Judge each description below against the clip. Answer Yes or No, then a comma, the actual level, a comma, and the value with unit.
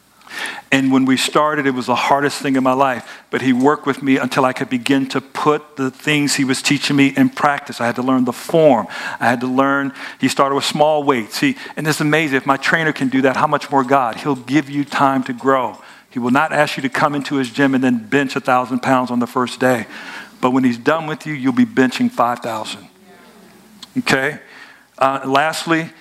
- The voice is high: No, low, 135 Hz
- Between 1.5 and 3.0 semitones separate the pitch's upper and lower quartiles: Yes, narrow, 2.6 semitones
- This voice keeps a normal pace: No, fast, 230 wpm